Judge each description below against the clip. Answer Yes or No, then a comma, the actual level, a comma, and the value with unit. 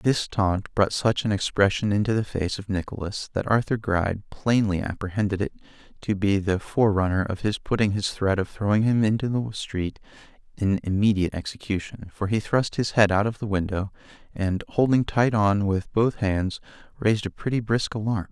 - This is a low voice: Yes, low, 105 Hz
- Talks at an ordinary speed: Yes, average, 185 wpm